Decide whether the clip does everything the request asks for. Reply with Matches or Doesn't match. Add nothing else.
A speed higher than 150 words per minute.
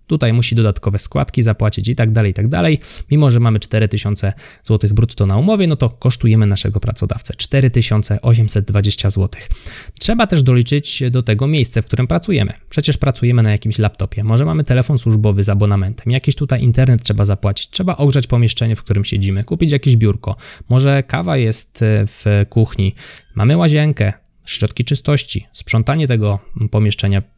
Matches